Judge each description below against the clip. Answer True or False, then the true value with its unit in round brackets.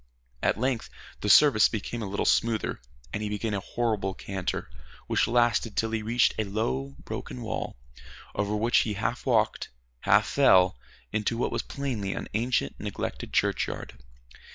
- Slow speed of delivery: False (155 wpm)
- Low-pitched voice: True (110 Hz)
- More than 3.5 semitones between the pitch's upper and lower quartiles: False (2.9 semitones)